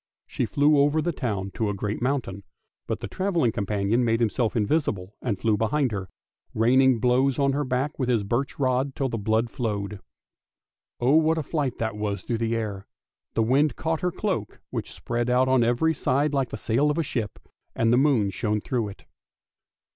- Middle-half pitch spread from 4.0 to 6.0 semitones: Yes, average, 4.4 semitones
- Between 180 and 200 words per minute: Yes, average, 195 wpm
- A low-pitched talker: Yes, low, 120 Hz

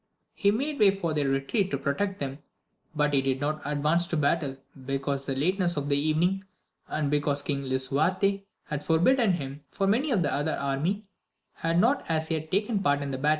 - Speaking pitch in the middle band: Yes, medium, 155 Hz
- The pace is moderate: Yes, average, 175 wpm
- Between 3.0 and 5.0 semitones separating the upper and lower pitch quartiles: No, wide, 5.4 semitones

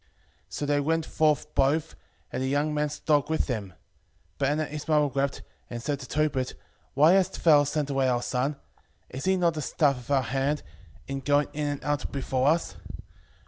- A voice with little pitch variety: Yes, narrow, 2.1 semitones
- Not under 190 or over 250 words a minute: Yes, average, 195 wpm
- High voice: No, medium, 145 Hz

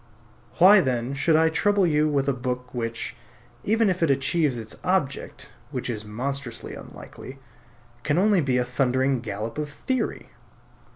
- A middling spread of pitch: Yes, average, 4.7 semitones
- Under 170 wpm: Yes, average, 155 wpm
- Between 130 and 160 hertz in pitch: Yes, medium, 140 Hz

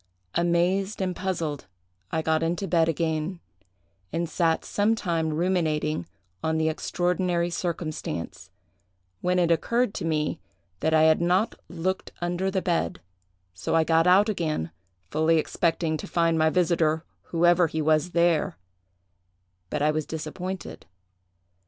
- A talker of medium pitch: Yes, medium, 165 Hz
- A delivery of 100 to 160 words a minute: Yes, slow, 135 wpm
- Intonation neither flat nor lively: No, narrow, 2.2 semitones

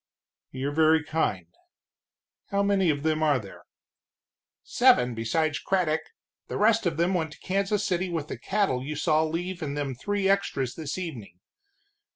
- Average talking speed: Yes, average, 160 wpm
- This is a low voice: No, medium, 160 Hz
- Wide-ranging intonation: No, average, 4.6 semitones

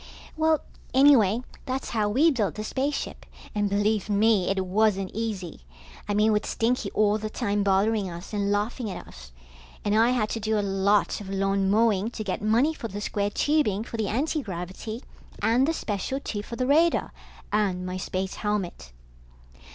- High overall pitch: Yes, high, 210 Hz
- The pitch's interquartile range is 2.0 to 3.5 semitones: Yes, average, 2.8 semitones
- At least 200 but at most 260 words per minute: No, average, 175 wpm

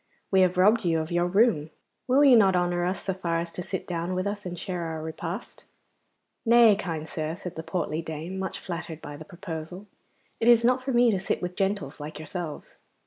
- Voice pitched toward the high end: No, medium, 180 Hz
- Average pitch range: Yes, average, 3.5 semitones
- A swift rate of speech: Yes, fast, 215 wpm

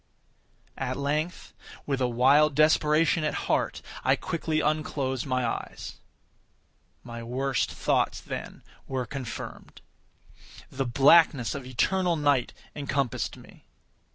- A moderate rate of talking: No, slow, 110 wpm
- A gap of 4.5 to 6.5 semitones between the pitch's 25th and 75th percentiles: No, average, 3.1 semitones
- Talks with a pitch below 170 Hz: Yes, medium, 140 Hz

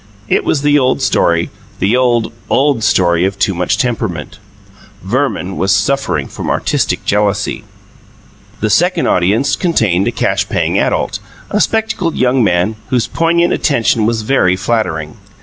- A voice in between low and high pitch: No, low, 110 Hz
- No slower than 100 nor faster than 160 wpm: Yes, average, 145 wpm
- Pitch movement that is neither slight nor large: No, wide, 6.6 semitones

